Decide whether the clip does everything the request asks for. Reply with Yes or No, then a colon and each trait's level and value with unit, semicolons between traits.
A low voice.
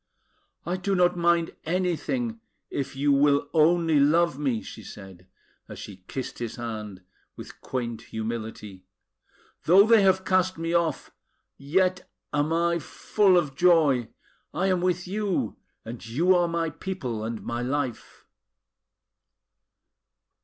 No: medium, 160 Hz